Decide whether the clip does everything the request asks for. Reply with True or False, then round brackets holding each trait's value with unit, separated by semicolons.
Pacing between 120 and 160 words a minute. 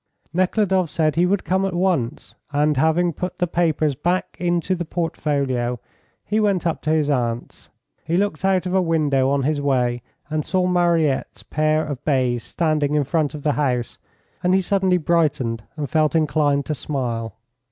False (175 wpm)